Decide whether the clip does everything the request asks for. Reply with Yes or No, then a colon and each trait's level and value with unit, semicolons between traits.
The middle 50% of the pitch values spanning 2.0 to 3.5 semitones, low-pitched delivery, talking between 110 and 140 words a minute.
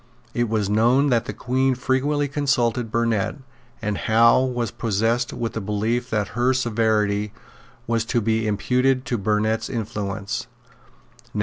Yes: average, 2.7 semitones; low, 115 Hz; slow, 135 wpm